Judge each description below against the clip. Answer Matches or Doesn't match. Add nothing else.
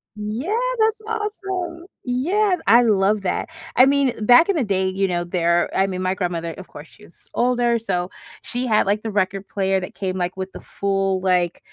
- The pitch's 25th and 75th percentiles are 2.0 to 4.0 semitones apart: Doesn't match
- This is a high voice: Matches